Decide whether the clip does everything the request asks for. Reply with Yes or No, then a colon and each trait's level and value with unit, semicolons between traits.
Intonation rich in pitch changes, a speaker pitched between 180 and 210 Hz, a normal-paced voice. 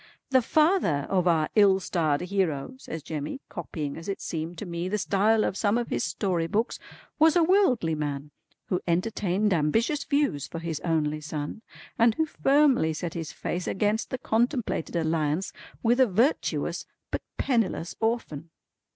Yes: wide, 6.4 semitones; medium, 185 Hz; average, 160 wpm